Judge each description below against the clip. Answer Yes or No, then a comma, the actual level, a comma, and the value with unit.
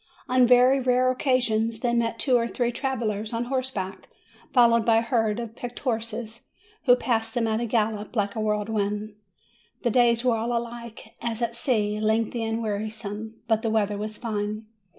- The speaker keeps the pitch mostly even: Yes, narrow, 1.8 semitones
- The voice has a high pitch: Yes, high, 230 Hz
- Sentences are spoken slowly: No, average, 175 wpm